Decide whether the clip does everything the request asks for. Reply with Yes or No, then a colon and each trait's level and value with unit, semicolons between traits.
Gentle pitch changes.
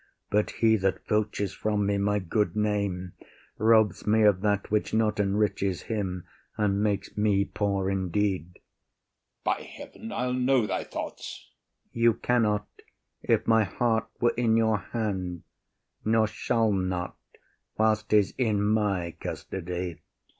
Yes: narrow, 2.2 semitones